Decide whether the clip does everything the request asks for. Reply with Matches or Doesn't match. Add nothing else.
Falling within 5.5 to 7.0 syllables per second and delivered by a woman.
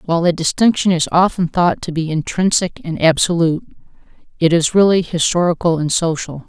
Matches